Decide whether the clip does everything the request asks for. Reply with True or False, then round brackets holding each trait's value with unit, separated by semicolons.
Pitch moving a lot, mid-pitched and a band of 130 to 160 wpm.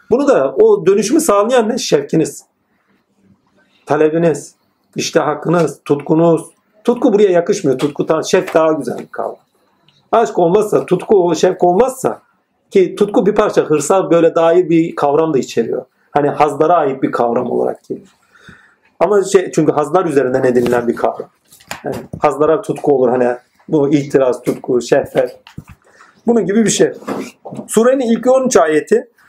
True (7.8 semitones; 170 Hz; 140 wpm)